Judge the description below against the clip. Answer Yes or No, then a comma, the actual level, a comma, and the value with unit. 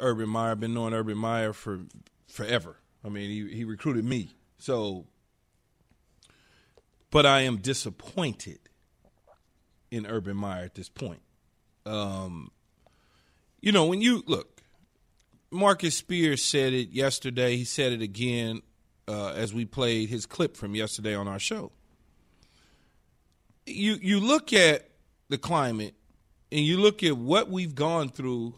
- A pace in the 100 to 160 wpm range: Yes, slow, 135 wpm